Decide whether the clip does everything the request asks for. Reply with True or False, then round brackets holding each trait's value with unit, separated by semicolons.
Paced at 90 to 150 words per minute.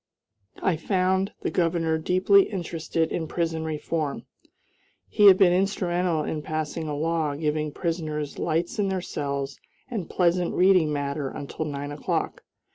True (140 wpm)